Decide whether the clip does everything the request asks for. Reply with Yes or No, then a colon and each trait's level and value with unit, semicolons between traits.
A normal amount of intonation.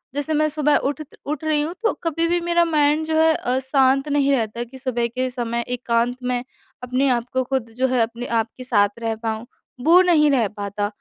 Yes: average, 4.2 semitones